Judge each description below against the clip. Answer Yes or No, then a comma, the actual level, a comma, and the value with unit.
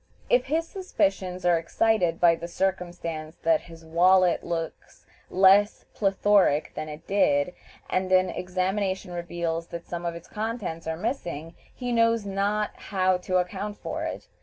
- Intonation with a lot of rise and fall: No, average, 3.2 semitones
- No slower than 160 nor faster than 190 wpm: No, average, 150 wpm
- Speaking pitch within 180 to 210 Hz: Yes, medium, 185 Hz